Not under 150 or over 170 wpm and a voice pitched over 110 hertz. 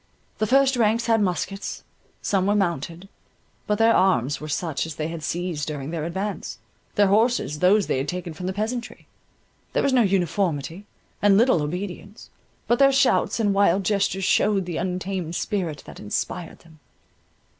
Yes: average, 165 wpm; high, 190 Hz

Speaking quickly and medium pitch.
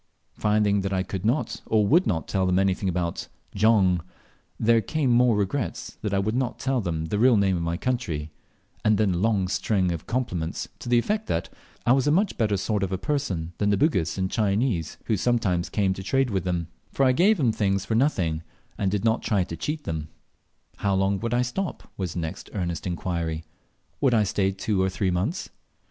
No: fast, 215 wpm; low, 100 Hz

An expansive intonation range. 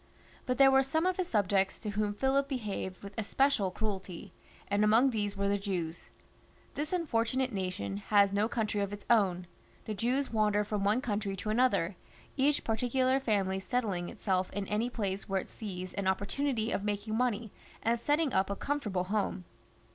No: average, 4.2 semitones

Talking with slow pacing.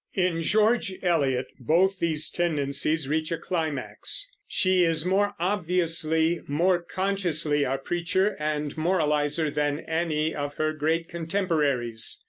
Yes: slow, 120 wpm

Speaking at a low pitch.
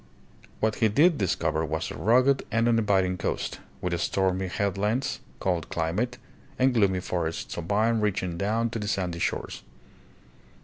Yes: low, 100 Hz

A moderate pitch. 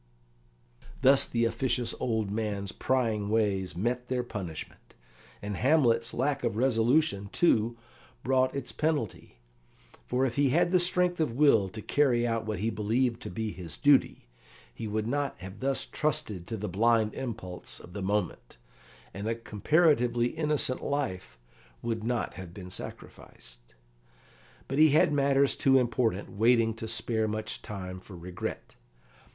No: low, 115 Hz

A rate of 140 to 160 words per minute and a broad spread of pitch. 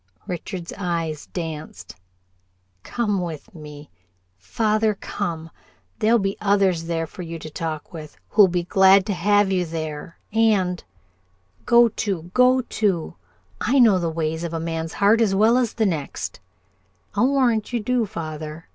No: average, 155 wpm; average, 4.7 semitones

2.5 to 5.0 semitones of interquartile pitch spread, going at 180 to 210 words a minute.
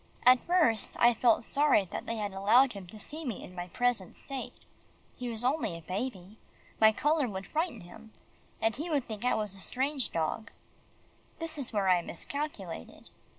No: wide, 5.6 semitones; average, 185 wpm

